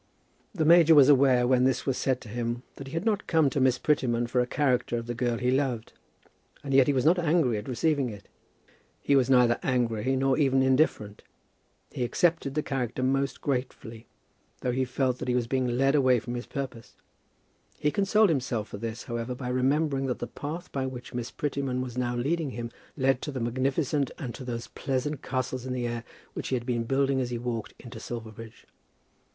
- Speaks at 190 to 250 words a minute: Yes, fast, 205 wpm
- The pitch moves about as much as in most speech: No, narrow, 2.3 semitones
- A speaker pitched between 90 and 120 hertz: No, low, 130 Hz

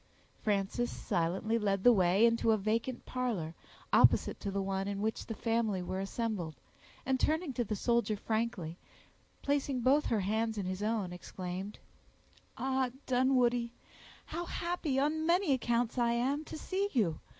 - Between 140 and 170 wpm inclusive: Yes, average, 155 wpm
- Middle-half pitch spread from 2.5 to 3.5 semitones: No, average, 4.7 semitones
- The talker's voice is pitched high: Yes, high, 230 Hz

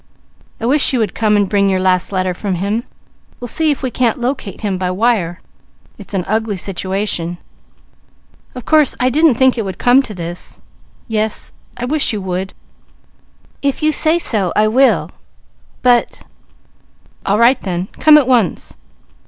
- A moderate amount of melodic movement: Yes, average, 5.0 semitones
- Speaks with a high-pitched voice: Yes, high, 215 Hz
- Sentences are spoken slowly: No, average, 165 wpm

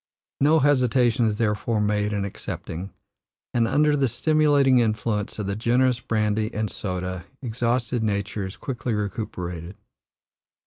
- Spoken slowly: Yes, slow, 130 wpm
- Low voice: Yes, low, 110 Hz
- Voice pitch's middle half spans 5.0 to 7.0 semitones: No, average, 3.4 semitones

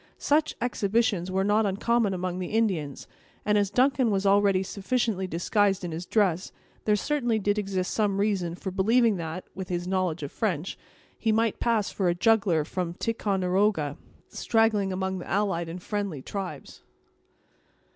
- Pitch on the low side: No, high, 195 Hz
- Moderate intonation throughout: Yes, average, 3.0 semitones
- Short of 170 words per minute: Yes, average, 155 wpm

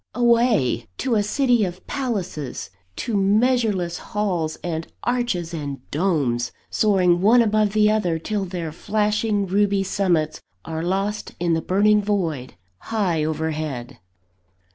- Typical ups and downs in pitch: Yes, average, 4.7 semitones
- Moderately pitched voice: No, high, 195 Hz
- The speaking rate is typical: No, slow, 120 wpm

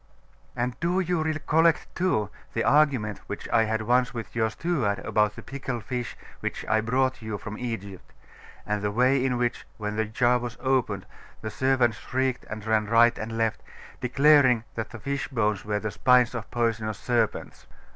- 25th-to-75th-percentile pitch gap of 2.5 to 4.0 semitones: Yes, average, 3.2 semitones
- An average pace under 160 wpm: No, average, 175 wpm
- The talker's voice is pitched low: Yes, low, 120 Hz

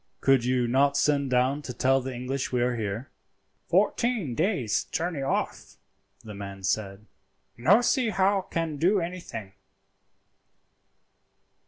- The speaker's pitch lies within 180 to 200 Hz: No, low, 135 Hz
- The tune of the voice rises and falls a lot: Yes, wide, 5.9 semitones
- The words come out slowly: Yes, slow, 130 wpm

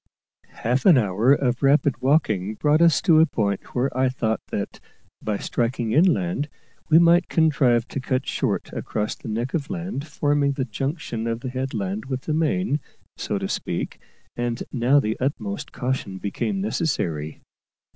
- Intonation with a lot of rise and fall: No, average, 4.8 semitones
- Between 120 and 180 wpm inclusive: Yes, average, 160 wpm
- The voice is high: No, low, 130 Hz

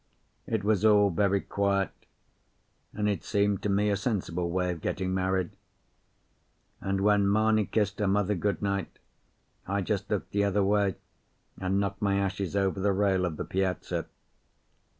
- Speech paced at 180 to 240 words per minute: No, average, 160 wpm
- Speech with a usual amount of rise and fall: No, narrow, 1.3 semitones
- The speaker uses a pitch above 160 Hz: No, low, 100 Hz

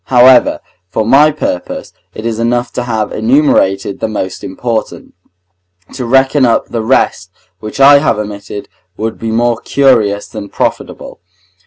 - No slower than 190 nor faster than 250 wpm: No, average, 145 wpm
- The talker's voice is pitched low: Yes, low, 115 Hz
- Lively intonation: No, average, 3.4 semitones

